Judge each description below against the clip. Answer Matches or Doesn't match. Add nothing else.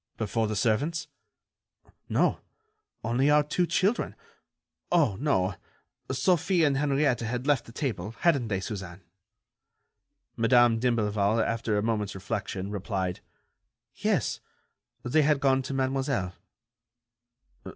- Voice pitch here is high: Doesn't match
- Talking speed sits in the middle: Doesn't match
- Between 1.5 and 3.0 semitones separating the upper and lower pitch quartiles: Doesn't match